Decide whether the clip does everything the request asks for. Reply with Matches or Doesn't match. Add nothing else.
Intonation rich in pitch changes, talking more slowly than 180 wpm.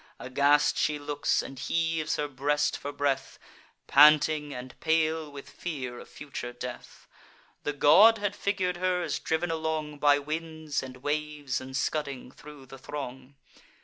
Doesn't match